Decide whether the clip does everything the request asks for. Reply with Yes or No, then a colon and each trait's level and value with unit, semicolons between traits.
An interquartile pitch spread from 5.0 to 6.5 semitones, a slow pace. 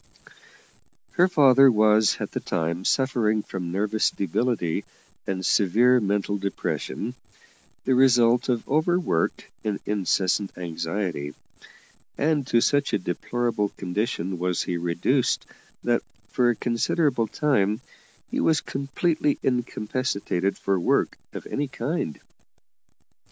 Yes: wide, 5.5 semitones; slow, 115 wpm